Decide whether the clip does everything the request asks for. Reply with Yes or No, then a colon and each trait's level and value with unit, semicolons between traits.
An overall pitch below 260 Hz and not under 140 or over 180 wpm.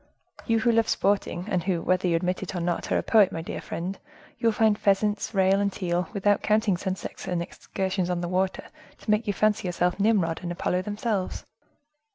No: high, 190 Hz; fast, 205 wpm